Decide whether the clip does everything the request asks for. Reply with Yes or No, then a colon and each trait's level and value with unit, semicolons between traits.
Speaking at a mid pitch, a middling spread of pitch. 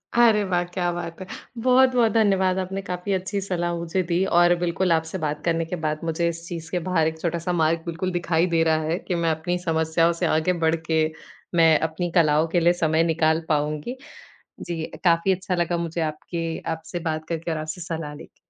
No: medium, 170 Hz; narrow, 2.0 semitones